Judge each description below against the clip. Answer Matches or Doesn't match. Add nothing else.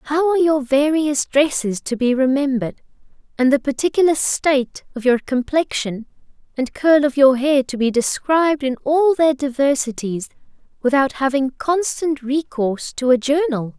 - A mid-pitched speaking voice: Doesn't match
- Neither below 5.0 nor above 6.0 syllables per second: Doesn't match